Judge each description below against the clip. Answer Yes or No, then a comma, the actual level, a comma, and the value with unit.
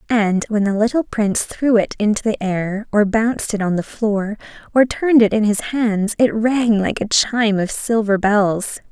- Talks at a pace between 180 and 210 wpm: Yes, average, 200 wpm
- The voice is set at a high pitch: Yes, high, 215 Hz